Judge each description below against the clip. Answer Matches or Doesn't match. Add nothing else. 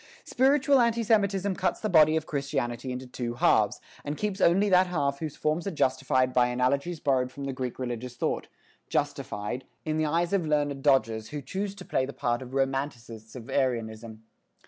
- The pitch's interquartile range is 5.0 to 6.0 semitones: Matches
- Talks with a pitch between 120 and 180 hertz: Matches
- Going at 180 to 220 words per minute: Matches